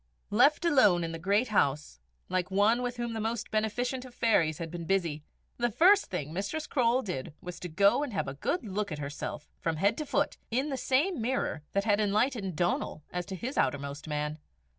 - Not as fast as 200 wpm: No, fast, 205 wpm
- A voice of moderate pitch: No, high, 205 Hz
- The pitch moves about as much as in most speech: No, wide, 6.7 semitones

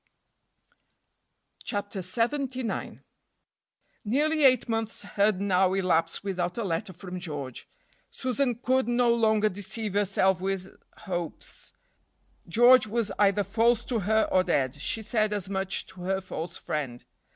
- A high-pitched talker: Yes, high, 205 Hz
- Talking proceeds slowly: Yes, slow, 130 wpm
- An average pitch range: Yes, average, 4.0 semitones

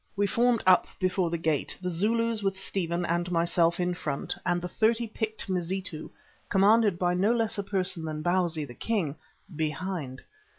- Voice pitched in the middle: Yes, medium, 180 Hz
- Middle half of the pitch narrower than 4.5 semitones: Yes, average, 3.2 semitones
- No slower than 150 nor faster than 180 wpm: Yes, average, 170 wpm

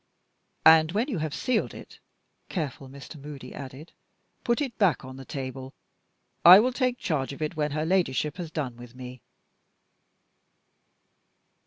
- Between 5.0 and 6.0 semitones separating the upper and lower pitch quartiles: Yes, wide, 5.5 semitones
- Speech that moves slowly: No, average, 150 wpm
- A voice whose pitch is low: No, medium, 150 Hz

